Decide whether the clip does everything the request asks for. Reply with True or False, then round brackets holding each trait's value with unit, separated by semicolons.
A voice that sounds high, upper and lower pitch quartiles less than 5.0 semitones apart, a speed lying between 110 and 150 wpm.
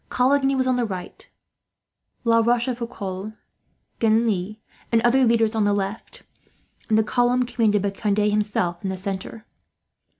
True (220 Hz; 2.9 semitones; 140 wpm)